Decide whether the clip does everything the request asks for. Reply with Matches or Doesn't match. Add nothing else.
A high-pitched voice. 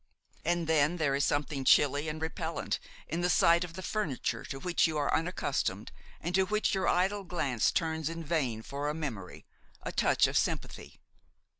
Doesn't match